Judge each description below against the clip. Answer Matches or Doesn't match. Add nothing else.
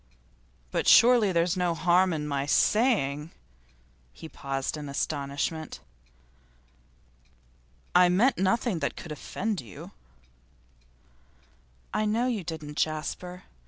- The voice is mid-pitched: Matches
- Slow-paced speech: Matches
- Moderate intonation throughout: Matches